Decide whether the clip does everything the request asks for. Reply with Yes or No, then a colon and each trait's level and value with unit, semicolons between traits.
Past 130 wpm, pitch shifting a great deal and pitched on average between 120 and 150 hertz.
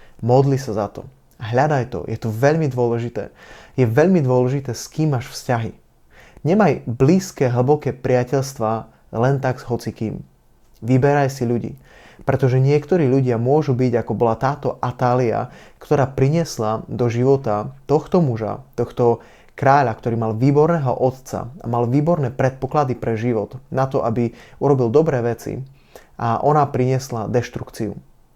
No: average, 140 wpm; average, 2.9 semitones; low, 130 Hz